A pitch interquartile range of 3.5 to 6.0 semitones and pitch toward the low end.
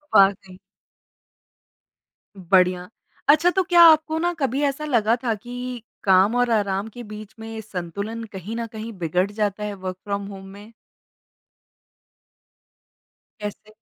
No: average, 4.1 semitones; high, 215 Hz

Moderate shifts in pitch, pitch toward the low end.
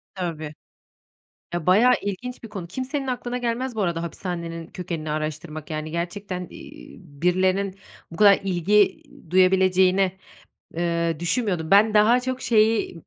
No: average, 3.9 semitones; medium, 185 Hz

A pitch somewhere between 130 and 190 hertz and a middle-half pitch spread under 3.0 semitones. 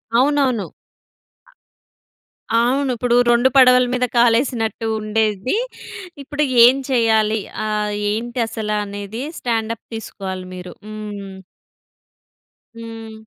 No: high, 225 Hz; narrow, 2.6 semitones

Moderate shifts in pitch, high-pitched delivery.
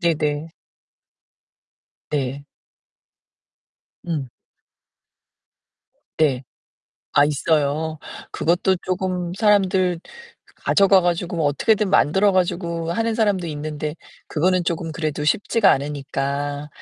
No: average, 4.0 semitones; medium, 165 Hz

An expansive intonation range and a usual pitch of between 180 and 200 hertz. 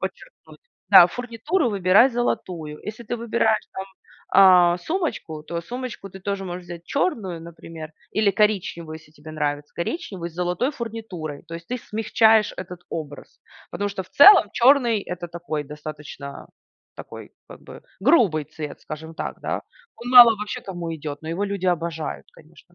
Yes: wide, 5.9 semitones; medium, 185 Hz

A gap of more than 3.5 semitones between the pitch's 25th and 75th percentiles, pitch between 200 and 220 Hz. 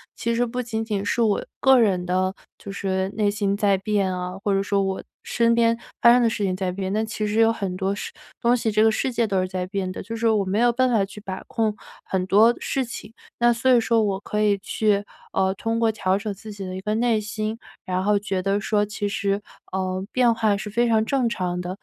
No: average, 2.9 semitones; high, 210 Hz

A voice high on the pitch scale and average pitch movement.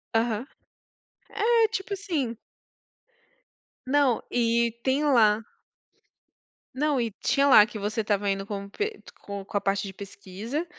No: high, 230 Hz; wide, 5.9 semitones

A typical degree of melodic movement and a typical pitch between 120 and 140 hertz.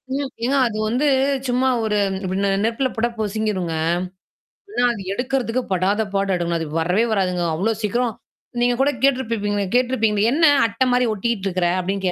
No: average, 4.1 semitones; high, 220 Hz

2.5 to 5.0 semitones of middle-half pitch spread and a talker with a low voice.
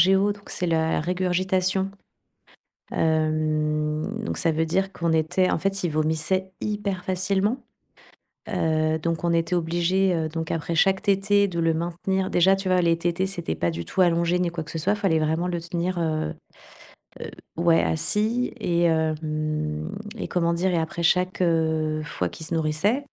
No: average, 2.9 semitones; medium, 170 Hz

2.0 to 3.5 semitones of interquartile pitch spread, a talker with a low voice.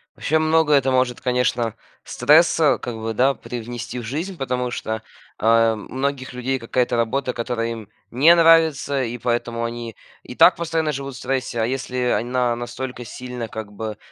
Yes: average, 2.8 semitones; low, 125 Hz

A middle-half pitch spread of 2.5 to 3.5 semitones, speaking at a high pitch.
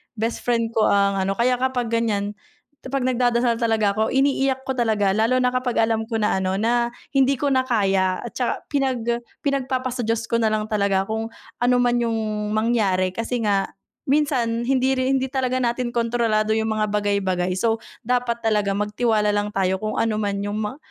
Yes: average, 3.1 semitones; high, 230 Hz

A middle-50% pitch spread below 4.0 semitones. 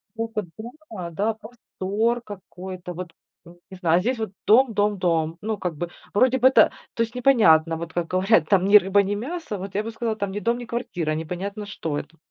No: average, 4.3 semitones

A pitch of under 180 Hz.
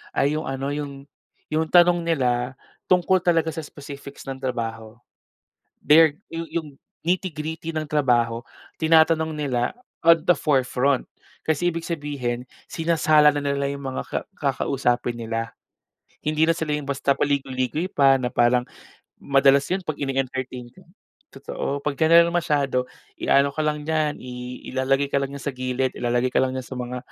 Yes: medium, 140 Hz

